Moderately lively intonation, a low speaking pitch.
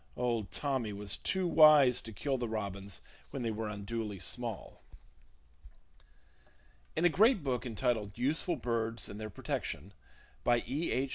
Yes: average, 4.4 semitones; low, 120 Hz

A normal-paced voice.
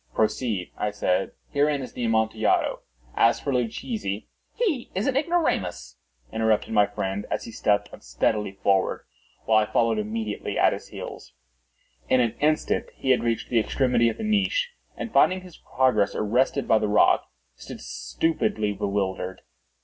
Yes: average, 155 wpm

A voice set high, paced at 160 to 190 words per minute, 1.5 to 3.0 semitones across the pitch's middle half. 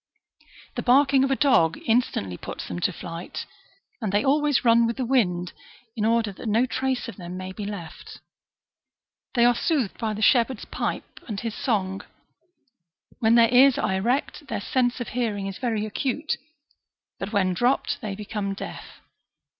No: high, 225 Hz; average, 170 wpm; average, 4.2 semitones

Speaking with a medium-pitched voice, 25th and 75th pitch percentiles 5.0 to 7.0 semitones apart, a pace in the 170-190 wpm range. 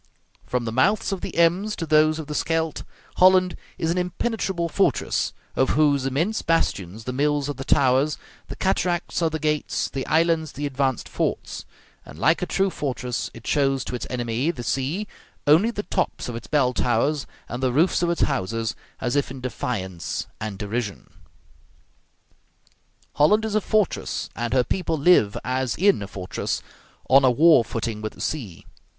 Yes: medium, 145 Hz; wide, 5.5 semitones; average, 175 wpm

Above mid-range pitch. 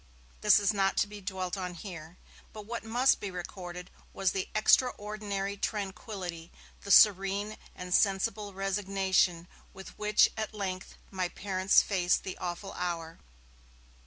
Yes: high, 195 Hz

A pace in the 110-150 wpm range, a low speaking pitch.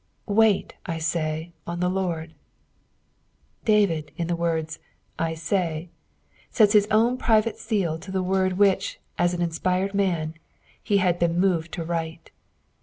No: slow, 135 wpm; medium, 175 Hz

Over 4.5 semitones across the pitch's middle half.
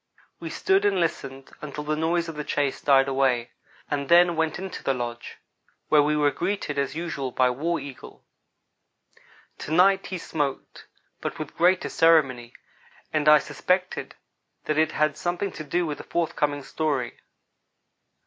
No: average, 3.6 semitones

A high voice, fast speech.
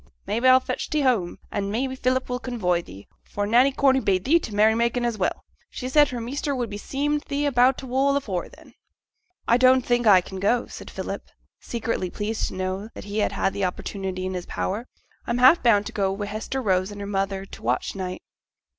Yes: high, 225 Hz; fast, 225 wpm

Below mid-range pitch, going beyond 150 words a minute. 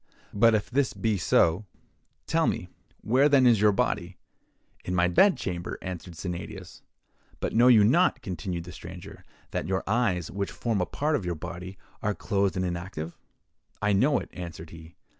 Yes: very low, 95 Hz; average, 165 wpm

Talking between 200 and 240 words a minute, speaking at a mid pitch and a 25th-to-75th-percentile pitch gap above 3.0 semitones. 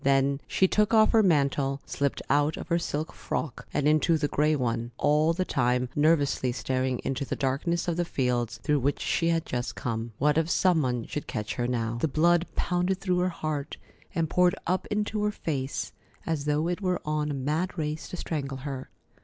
Yes: fast, 205 wpm; medium, 150 Hz; average, 4.2 semitones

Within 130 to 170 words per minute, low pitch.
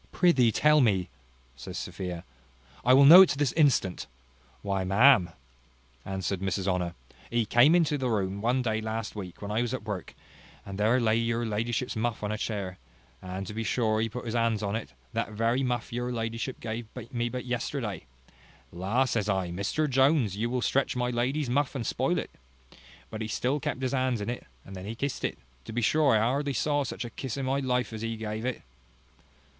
No: fast, 205 wpm; low, 115 Hz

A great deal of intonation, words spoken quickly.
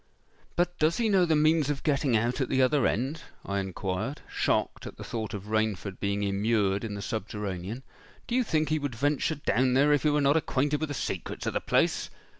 Yes: wide, 6.2 semitones; fast, 215 wpm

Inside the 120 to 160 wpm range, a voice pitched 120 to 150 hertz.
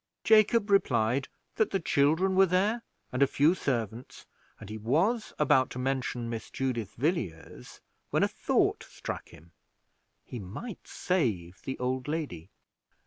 Yes: average, 140 wpm; low, 135 Hz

